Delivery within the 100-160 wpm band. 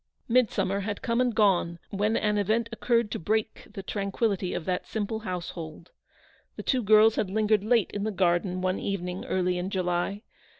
No: average, 175 wpm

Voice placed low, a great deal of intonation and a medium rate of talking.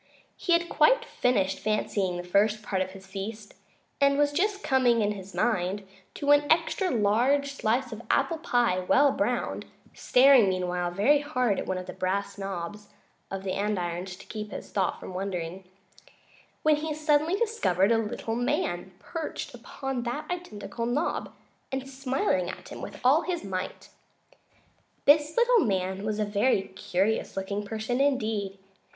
No: high, 220 Hz; wide, 6.6 semitones; average, 160 wpm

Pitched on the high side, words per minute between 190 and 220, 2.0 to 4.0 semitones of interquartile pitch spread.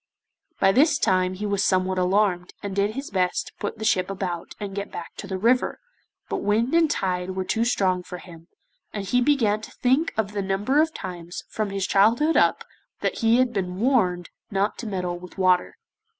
Yes: high, 195 Hz; fast, 205 wpm; average, 3.4 semitones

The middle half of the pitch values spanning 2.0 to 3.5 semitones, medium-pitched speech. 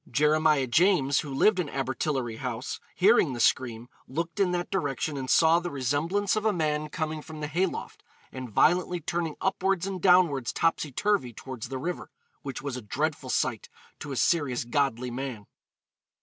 No: average, 5.1 semitones; medium, 150 Hz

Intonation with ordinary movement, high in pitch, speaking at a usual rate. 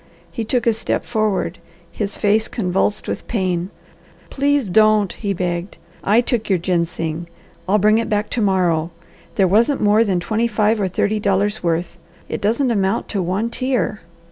Yes: average, 3.3 semitones; high, 205 Hz; average, 170 wpm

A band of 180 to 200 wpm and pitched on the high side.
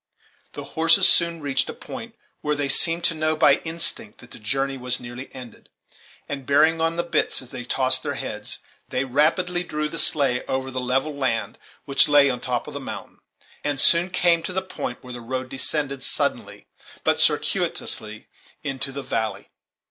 No: average, 185 wpm; medium, 140 Hz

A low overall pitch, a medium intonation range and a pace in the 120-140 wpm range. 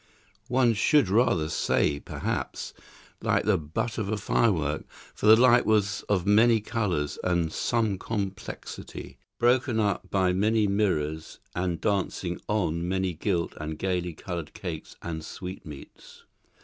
Yes: very low, 95 Hz; average, 4.3 semitones; slow, 135 wpm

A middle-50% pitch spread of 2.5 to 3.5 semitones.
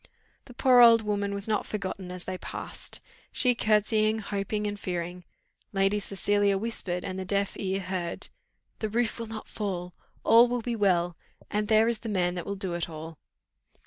Yes: average, 2.9 semitones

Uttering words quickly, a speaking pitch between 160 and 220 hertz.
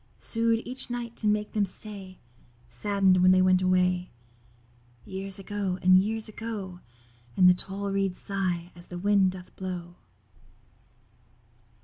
No: slow, 135 wpm; high, 190 Hz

